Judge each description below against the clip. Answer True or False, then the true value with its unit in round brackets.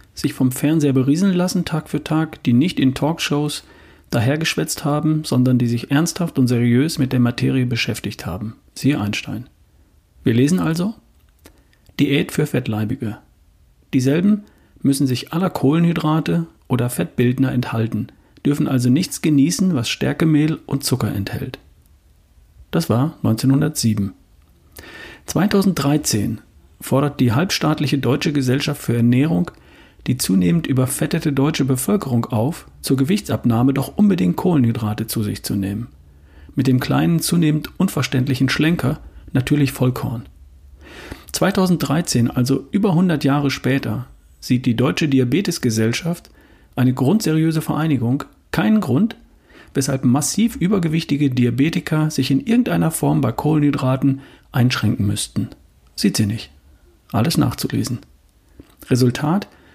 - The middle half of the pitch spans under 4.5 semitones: False (4.8 semitones)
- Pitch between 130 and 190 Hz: True (135 Hz)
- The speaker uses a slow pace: True (120 wpm)